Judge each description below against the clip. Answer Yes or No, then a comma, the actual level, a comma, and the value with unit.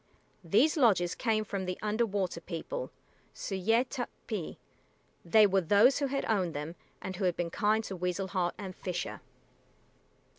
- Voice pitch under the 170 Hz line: No, high, 195 Hz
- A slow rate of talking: No, average, 155 wpm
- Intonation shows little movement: No, average, 3.6 semitones